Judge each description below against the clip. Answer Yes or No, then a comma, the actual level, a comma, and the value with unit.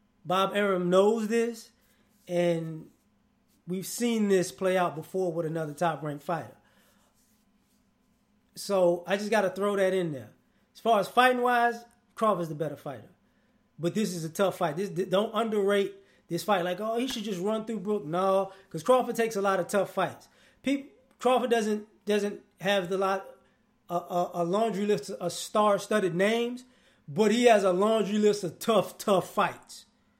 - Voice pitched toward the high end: Yes, high, 200 Hz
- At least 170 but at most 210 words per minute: Yes, average, 175 wpm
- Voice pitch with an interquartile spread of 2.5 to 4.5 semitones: Yes, average, 3.4 semitones